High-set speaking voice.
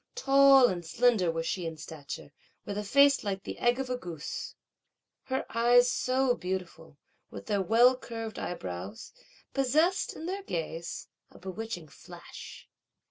Yes: high, 220 Hz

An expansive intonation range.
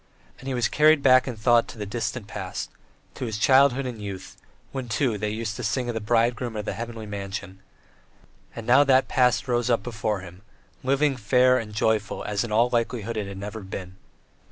No: average, 3.3 semitones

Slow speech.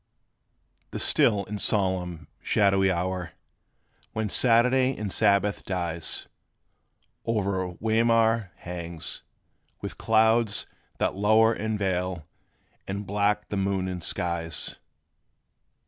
Yes: slow, 100 wpm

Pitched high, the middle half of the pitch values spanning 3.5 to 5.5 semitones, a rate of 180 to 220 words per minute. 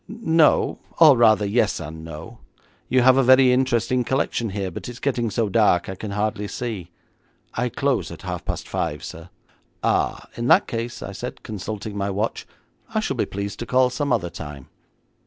No: low, 115 Hz; average, 4.2 semitones; average, 185 wpm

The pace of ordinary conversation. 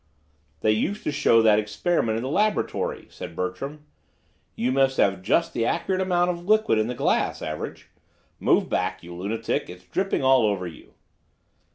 Yes: average, 175 wpm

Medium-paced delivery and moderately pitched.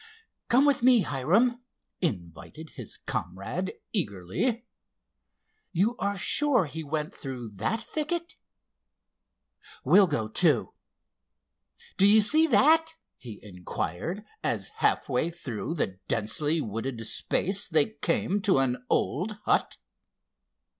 No: slow, 115 wpm; medium, 165 Hz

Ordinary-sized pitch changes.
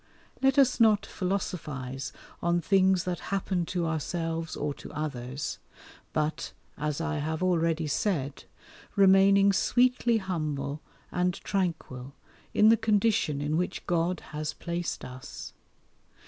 Yes: average, 4.4 semitones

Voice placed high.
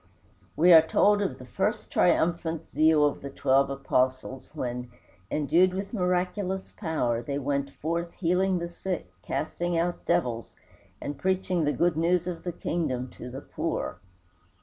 No: medium, 165 Hz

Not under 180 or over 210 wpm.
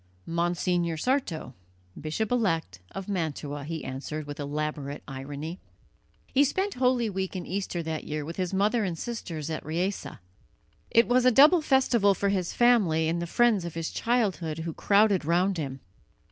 No: average, 160 wpm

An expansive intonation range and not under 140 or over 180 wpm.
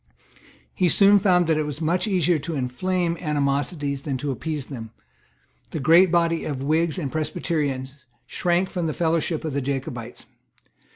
No: average, 3.7 semitones; average, 160 wpm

